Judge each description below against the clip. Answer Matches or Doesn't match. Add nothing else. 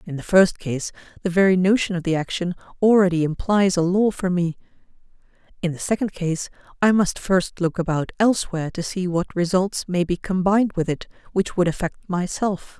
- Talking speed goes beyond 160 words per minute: Matches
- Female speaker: Matches